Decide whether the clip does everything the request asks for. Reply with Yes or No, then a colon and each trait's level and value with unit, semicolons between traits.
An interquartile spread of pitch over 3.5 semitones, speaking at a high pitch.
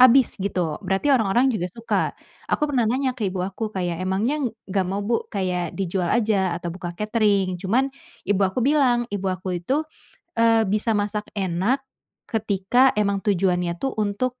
Yes: average, 4.0 semitones; high, 205 Hz